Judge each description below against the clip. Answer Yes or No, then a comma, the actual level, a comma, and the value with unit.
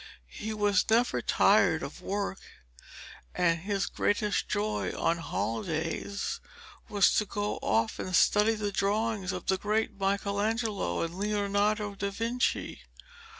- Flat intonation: Yes, narrow, 1.8 semitones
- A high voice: Yes, high, 205 Hz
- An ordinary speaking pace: No, slow, 125 wpm